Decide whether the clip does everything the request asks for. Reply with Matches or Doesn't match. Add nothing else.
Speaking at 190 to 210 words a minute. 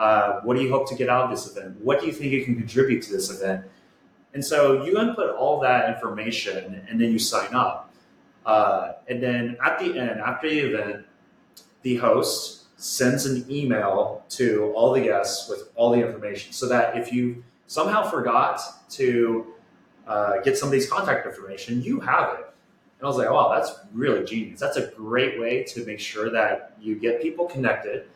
Matches